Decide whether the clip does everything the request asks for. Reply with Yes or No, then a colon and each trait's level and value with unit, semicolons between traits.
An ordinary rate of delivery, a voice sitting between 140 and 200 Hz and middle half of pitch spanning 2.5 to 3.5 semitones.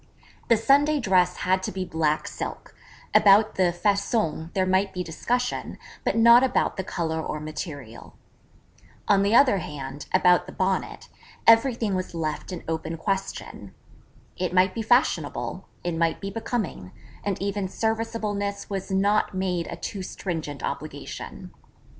No: average, 145 wpm; high, 190 Hz; average, 4.0 semitones